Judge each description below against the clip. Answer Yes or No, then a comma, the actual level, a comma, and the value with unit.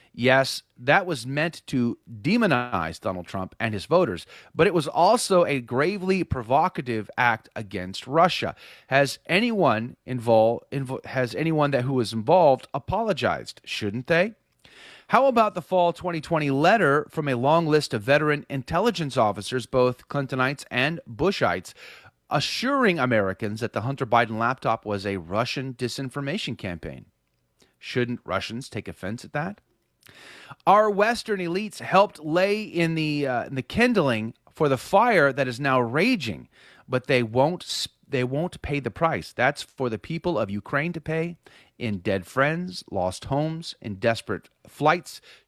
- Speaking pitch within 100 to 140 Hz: Yes, low, 135 Hz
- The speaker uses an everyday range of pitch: No, wide, 6.0 semitones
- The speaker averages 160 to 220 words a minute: No, average, 150 wpm